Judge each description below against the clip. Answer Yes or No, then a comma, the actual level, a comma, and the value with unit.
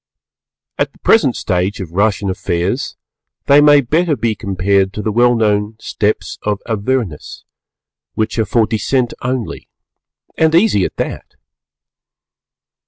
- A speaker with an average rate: No, slow, 130 wpm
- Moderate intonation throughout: Yes, average, 4.3 semitones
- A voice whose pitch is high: No, low, 110 Hz